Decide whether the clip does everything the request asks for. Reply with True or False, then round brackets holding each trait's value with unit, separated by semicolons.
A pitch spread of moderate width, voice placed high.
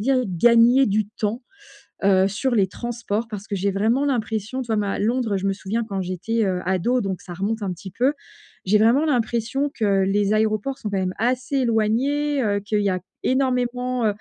True (3.9 semitones; 220 Hz)